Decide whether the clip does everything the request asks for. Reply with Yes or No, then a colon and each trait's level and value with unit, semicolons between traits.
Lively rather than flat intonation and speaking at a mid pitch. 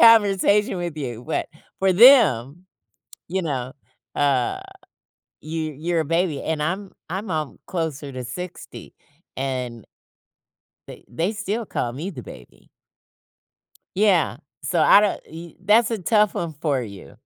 Yes: wide, 5.9 semitones; medium, 165 Hz